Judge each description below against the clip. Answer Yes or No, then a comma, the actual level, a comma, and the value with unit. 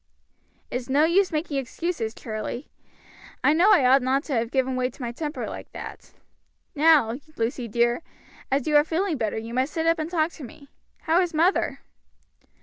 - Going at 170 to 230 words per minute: Yes, average, 185 wpm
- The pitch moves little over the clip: No, average, 4.7 semitones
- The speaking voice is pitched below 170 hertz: No, very high, 280 Hz